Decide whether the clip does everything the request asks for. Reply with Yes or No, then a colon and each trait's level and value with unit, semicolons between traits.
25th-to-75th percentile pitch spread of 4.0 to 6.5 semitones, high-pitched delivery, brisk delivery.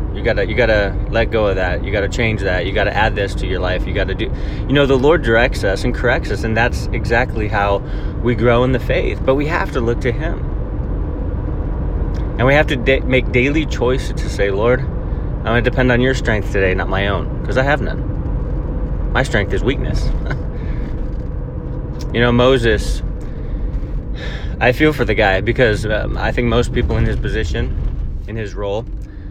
No: average, 4.4 semitones; low, 110 Hz; fast, 210 wpm